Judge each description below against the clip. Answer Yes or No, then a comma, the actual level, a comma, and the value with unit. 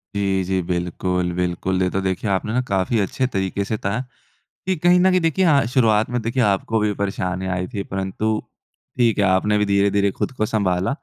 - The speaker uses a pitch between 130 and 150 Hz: No, low, 100 Hz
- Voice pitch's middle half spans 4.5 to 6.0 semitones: No, average, 3.1 semitones